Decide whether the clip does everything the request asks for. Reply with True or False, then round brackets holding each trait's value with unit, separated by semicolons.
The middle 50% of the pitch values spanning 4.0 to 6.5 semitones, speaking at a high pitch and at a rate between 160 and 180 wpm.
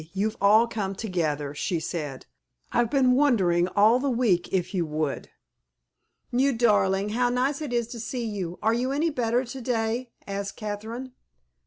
True (4.5 semitones; 220 Hz; 165 wpm)